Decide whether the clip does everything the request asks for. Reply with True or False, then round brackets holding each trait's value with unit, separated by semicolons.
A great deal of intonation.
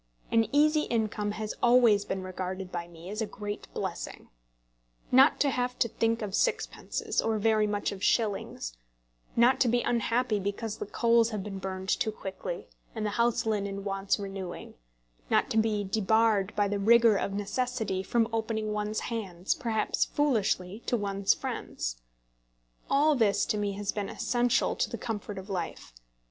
False (2.8 semitones)